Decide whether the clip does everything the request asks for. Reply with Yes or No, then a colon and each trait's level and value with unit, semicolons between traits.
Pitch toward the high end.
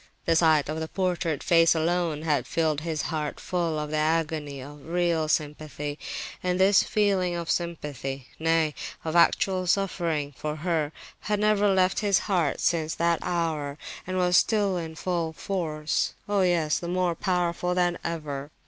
No: medium, 165 Hz